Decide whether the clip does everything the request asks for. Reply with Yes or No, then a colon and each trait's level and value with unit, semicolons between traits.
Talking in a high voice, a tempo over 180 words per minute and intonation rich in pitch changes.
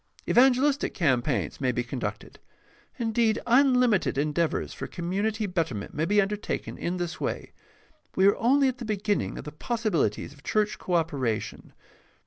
No: high, 195 Hz; average, 150 wpm; wide, 7.2 semitones